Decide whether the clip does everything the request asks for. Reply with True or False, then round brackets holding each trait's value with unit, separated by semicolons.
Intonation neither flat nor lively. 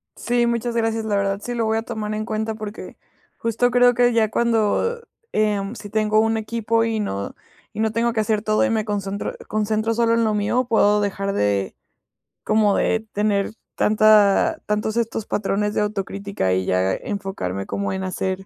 False (2.1 semitones)